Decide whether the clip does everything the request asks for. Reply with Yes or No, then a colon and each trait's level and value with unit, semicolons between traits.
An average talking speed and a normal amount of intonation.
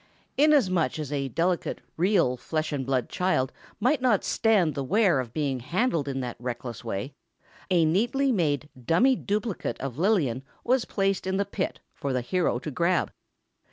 No: average, 165 wpm; wide, 7.0 semitones